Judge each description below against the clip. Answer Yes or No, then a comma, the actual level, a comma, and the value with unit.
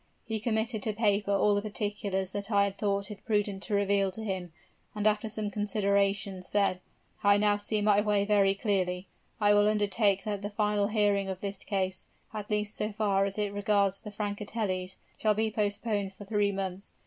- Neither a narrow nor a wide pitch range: No, narrow, 1.1 semitones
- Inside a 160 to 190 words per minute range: Yes, average, 185 wpm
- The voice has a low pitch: No, high, 205 Hz